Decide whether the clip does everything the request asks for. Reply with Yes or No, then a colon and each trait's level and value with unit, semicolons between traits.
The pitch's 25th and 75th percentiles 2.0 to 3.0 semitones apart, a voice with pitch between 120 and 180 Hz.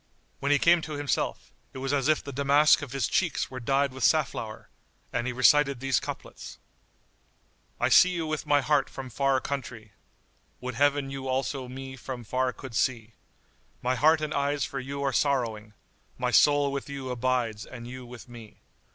Yes: narrow, 2.4 semitones; low, 135 Hz